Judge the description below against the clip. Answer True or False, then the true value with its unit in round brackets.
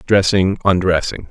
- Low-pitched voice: True (95 Hz)